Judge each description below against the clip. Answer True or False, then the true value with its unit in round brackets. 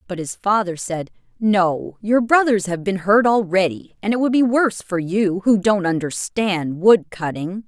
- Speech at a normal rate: True (180 wpm)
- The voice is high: True (195 Hz)